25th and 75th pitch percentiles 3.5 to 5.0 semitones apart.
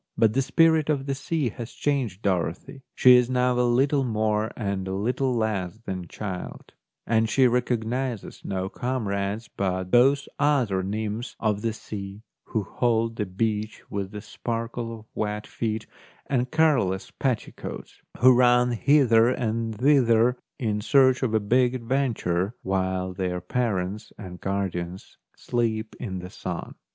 Yes: average, 4.0 semitones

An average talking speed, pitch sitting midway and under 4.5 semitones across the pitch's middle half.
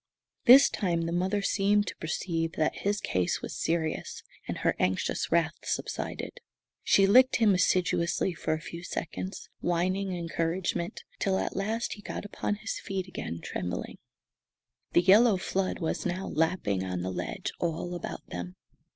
Yes: average, 155 wpm; medium, 180 Hz; average, 3.3 semitones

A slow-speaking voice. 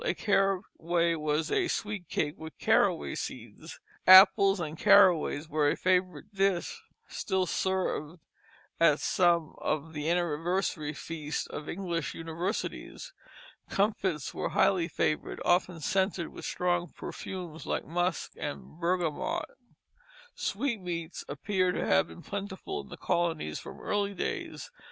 Yes: slow, 125 wpm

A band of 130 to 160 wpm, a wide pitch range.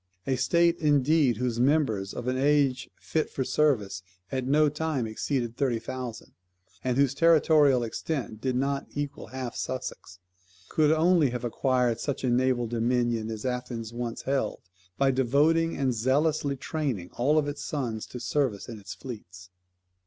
No: average, 155 wpm; average, 3.5 semitones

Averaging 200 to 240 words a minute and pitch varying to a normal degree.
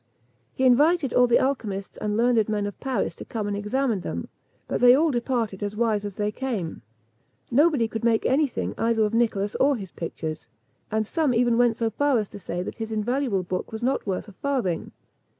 Yes: fast, 205 wpm; average, 3.7 semitones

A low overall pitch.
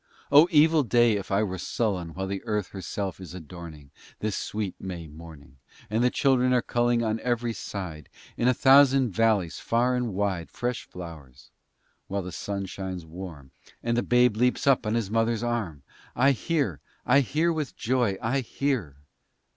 Yes: low, 110 Hz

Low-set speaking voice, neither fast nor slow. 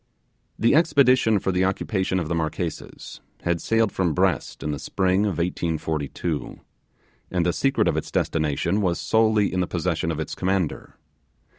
Yes: very low, 90 Hz; average, 160 wpm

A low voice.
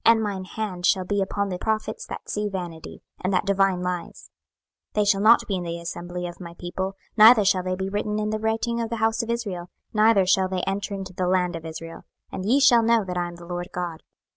No: high, 190 Hz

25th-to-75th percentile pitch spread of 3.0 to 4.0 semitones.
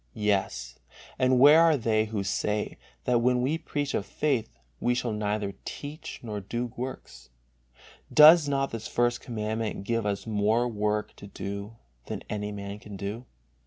Yes: average, 3.4 semitones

